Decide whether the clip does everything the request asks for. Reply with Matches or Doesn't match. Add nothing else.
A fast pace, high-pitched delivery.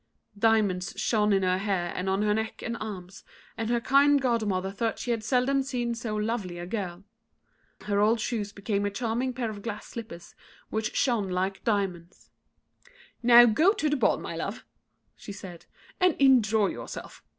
Doesn't match